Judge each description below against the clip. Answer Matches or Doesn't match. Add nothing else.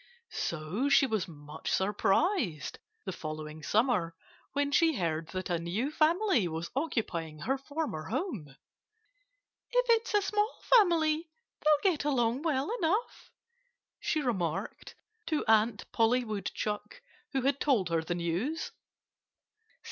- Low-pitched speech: Doesn't match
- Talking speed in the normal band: Doesn't match